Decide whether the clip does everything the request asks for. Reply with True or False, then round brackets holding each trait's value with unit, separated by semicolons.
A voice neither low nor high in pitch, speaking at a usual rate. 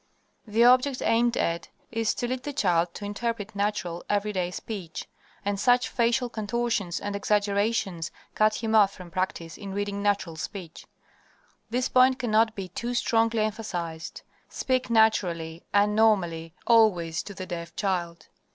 False (205 Hz; 145 wpm)